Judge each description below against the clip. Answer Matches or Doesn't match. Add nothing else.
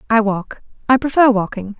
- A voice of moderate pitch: Doesn't match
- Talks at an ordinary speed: Matches